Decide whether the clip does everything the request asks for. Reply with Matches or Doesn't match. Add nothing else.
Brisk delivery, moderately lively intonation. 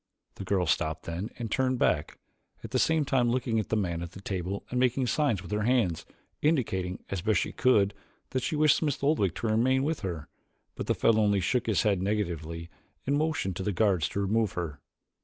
Doesn't match